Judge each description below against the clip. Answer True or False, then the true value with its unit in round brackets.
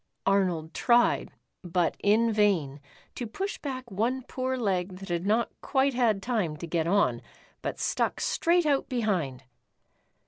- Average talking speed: True (145 wpm)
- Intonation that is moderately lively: False (5.9 semitones)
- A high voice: True (210 Hz)